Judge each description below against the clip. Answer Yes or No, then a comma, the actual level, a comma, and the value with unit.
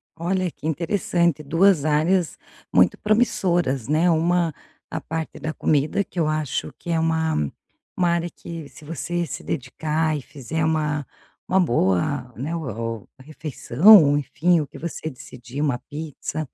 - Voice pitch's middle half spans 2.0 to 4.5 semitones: Yes, average, 2.8 semitones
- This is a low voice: No, medium, 160 Hz